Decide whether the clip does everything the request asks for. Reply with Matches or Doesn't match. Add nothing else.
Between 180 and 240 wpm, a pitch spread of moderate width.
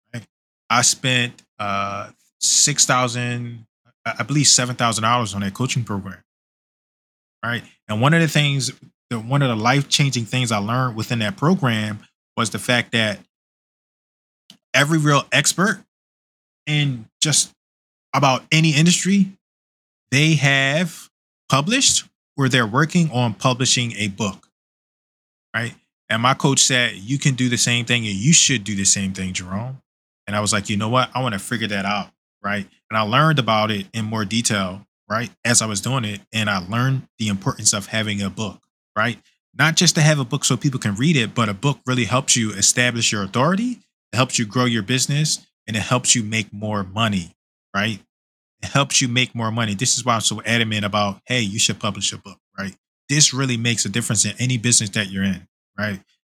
Matches